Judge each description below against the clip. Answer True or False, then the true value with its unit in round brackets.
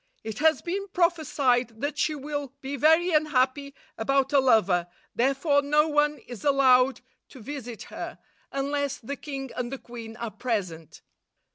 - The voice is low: False (275 Hz)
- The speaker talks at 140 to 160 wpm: True (150 wpm)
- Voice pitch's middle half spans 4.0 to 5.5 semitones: False (3.4 semitones)